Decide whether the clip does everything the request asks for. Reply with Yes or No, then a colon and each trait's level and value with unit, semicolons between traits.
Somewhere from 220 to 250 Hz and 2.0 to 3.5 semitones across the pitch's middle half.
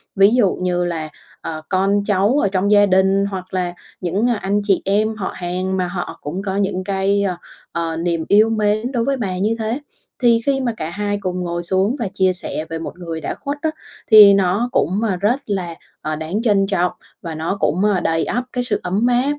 No: high, 195 Hz; average, 3.0 semitones